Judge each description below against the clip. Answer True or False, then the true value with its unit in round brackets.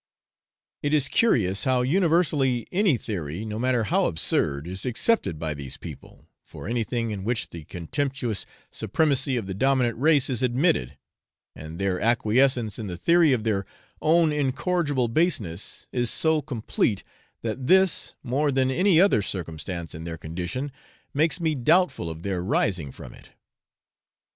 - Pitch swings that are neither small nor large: False (7.6 semitones)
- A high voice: False (120 Hz)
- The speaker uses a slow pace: False (150 wpm)